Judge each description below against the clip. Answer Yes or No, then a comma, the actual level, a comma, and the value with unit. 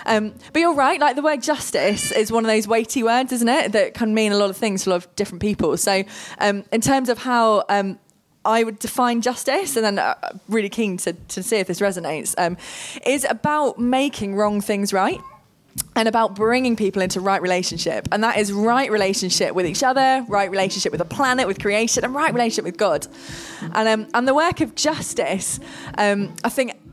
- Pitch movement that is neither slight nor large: Yes, average, 3.7 semitones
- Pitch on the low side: No, high, 220 Hz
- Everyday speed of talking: No, fast, 210 wpm